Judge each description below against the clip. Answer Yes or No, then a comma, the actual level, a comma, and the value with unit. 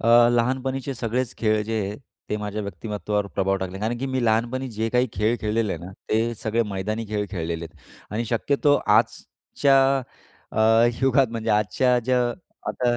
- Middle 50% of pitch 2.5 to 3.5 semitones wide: Yes, average, 3.0 semitones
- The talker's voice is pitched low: Yes, low, 115 Hz